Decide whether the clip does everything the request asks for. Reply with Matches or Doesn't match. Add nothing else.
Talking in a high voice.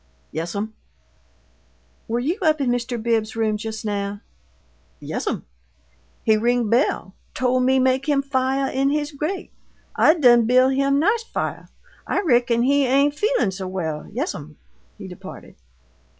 Matches